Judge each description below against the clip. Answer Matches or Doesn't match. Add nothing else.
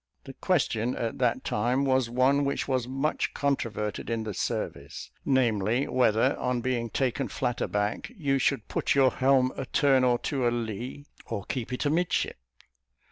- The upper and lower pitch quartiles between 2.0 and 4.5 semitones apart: Matches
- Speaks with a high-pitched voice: Doesn't match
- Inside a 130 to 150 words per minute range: Doesn't match